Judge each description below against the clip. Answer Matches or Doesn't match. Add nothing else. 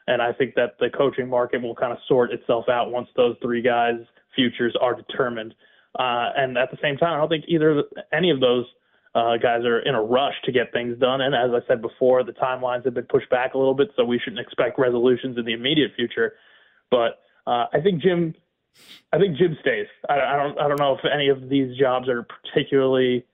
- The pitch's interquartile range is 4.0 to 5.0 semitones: Doesn't match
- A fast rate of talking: Matches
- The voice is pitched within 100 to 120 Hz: Doesn't match